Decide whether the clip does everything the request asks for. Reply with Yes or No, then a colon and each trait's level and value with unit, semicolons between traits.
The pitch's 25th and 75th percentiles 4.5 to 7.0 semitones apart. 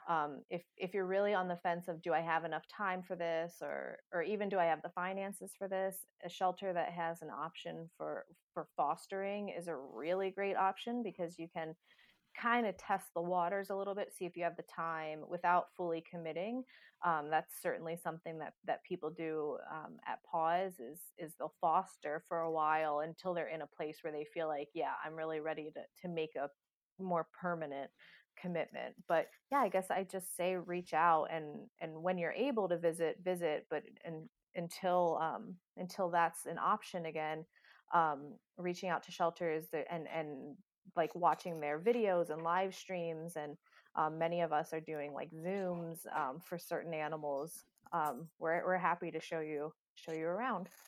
No: narrow, 2.6 semitones